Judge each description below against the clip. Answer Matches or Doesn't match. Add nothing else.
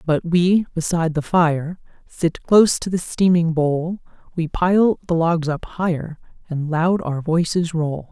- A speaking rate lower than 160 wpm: Doesn't match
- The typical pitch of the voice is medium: Matches